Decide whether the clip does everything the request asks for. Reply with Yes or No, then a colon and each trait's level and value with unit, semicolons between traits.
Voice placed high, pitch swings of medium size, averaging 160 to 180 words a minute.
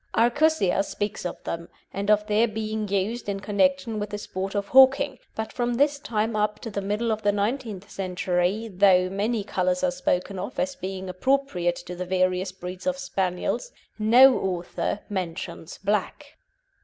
Yes: high, 205 Hz; average, 4.0 semitones; average, 170 wpm